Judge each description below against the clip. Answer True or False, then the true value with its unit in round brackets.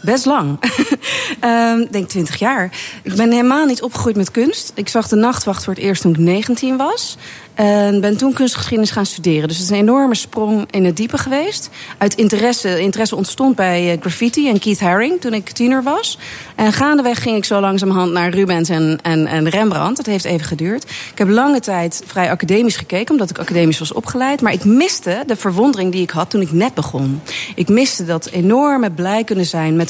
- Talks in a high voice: True (205 Hz)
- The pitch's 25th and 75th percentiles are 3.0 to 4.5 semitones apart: False (5.2 semitones)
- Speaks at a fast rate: True (205 wpm)